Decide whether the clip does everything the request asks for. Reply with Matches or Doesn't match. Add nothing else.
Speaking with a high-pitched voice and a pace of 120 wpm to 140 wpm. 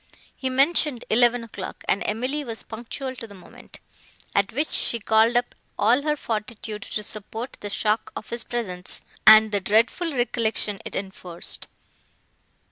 Doesn't match